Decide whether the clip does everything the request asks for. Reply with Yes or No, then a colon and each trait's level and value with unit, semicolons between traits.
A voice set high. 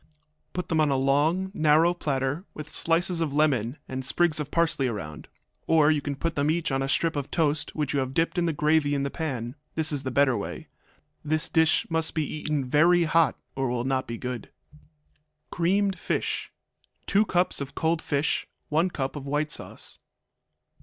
No: medium, 150 Hz